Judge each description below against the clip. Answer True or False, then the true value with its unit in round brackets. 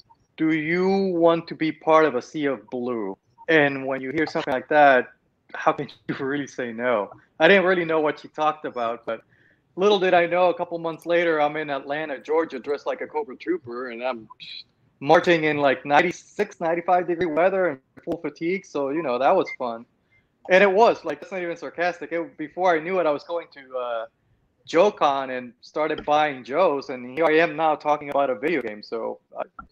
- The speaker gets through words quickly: True (210 wpm)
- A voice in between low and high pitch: True (155 Hz)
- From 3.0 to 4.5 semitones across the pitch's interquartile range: True (4.1 semitones)